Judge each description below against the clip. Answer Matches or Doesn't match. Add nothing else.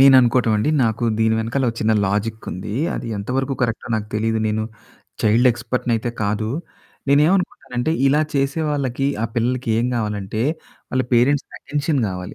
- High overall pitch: Doesn't match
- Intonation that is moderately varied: Matches